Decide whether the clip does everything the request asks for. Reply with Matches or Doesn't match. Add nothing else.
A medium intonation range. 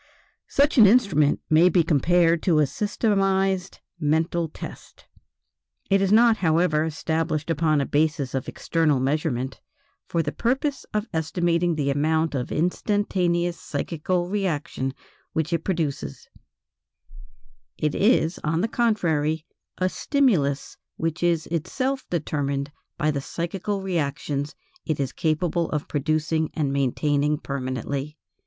Matches